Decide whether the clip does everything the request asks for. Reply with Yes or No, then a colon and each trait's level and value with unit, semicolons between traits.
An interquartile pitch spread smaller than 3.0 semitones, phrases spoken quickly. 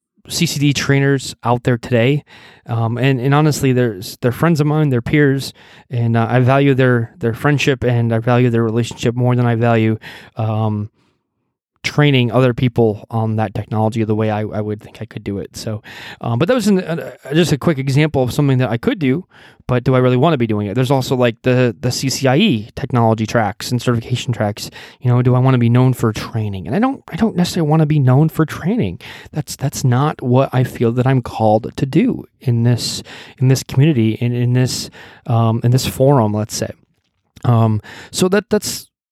No: average, 3.4 semitones; fast, 210 wpm